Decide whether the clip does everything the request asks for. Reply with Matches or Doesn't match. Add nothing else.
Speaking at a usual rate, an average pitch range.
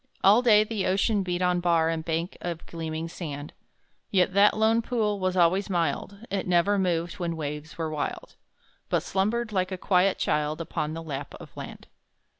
Matches